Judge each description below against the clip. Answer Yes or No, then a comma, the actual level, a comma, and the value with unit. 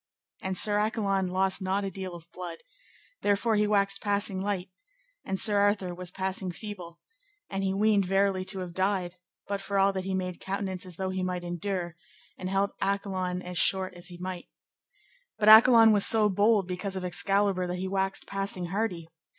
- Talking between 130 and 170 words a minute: No, average, 185 wpm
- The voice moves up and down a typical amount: No, narrow, 1.7 semitones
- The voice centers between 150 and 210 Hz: Yes, high, 190 Hz